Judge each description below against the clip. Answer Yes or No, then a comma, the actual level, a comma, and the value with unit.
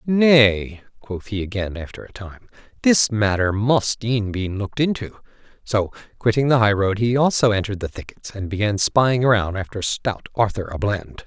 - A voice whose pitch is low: Yes, low, 110 Hz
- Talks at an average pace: Yes, average, 170 wpm